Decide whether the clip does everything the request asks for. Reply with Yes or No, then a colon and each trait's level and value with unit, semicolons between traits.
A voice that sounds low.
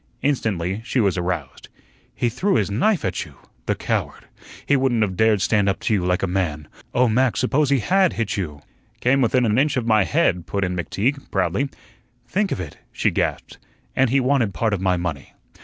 Yes: low, 110 Hz